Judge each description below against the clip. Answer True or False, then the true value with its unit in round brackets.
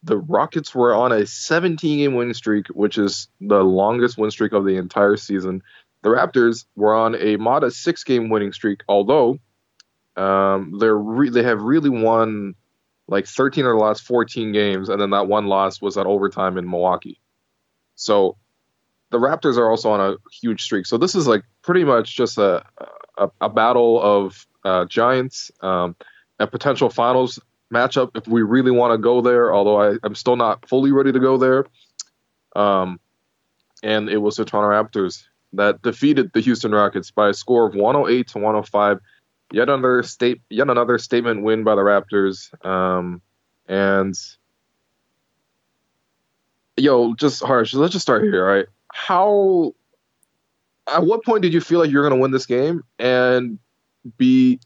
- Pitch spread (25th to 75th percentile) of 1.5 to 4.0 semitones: True (3.7 semitones)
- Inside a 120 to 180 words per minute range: True (170 wpm)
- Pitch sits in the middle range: False (110 Hz)